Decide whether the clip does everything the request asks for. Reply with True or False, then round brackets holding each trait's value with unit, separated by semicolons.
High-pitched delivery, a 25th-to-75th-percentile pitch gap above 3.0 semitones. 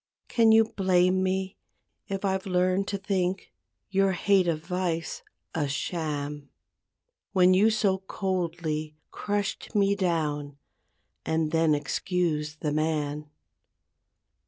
False (180 Hz; 3.8 semitones)